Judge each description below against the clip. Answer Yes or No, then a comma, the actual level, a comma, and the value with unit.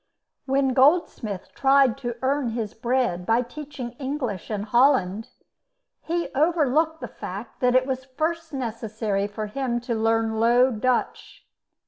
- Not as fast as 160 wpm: Yes, slow, 135 wpm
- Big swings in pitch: No, average, 3.7 semitones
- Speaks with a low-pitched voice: No, very high, 250 Hz